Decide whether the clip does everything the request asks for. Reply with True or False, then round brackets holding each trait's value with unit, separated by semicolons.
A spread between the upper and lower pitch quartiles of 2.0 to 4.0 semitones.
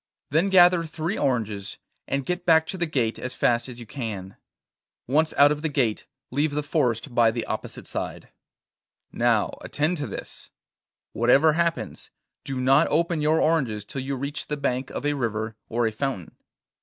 False (5.0 semitones)